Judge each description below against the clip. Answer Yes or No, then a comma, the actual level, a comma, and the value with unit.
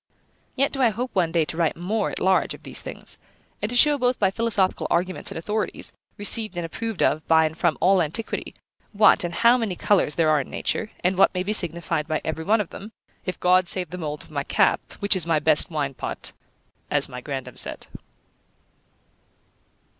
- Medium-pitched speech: Yes, medium, 180 Hz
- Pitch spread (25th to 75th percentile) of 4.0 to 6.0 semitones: Yes, average, 4.8 semitones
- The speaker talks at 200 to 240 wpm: Yes, fast, 205 wpm